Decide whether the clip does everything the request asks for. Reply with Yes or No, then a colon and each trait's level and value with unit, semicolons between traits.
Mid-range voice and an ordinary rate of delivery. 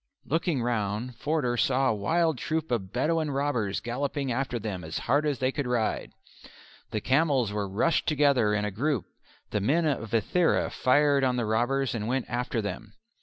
No: low, 125 Hz; average, 175 wpm